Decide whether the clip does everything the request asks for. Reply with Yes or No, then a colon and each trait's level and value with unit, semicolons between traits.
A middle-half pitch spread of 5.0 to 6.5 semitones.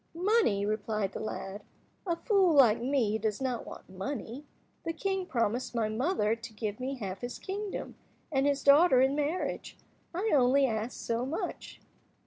Yes: wide, 5.6 semitones